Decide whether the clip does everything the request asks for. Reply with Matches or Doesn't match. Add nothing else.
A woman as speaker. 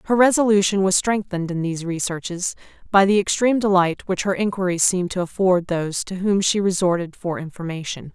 Matches